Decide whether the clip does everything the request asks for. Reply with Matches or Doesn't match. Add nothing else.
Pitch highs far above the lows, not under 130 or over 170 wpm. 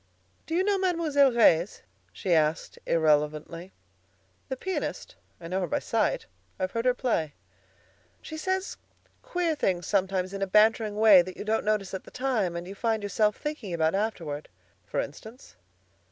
Matches